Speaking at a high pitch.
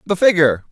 No: medium, 165 Hz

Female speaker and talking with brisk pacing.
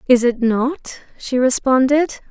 No: female; slow, 130 wpm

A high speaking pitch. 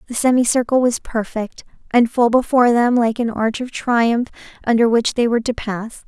Yes: high, 235 Hz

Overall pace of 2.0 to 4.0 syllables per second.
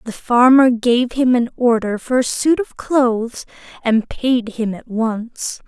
Yes: 3.7 syllables/s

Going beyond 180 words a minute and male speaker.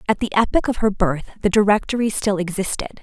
No: average, 200 wpm; female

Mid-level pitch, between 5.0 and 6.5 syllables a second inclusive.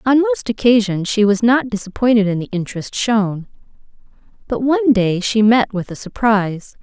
No: high, 220 Hz; 5.1 syllables/s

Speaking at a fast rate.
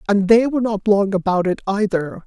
Yes: fast, 210 wpm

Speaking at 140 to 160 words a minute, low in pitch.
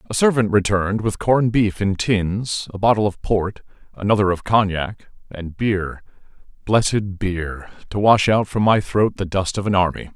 No: average, 175 wpm; low, 100 Hz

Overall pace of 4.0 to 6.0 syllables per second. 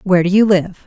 No: 6.5 syllables/s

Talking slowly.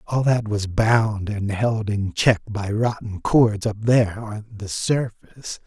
No: average, 170 wpm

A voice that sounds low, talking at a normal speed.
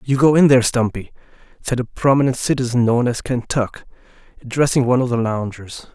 Yes: low, 125 Hz; average, 170 wpm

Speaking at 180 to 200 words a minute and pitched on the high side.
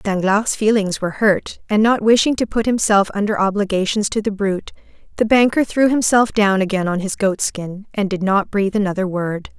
Yes: average, 195 wpm; high, 205 Hz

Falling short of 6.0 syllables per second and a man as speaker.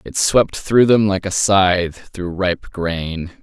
Yes: 3.5 syllables/s; male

